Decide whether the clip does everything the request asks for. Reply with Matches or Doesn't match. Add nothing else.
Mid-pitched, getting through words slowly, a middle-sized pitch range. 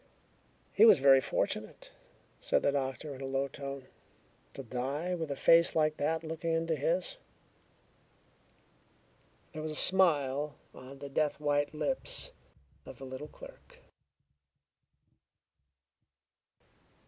Matches